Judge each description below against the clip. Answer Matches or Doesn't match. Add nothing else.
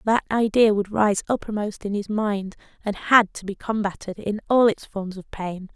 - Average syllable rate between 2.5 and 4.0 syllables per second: Doesn't match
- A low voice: Doesn't match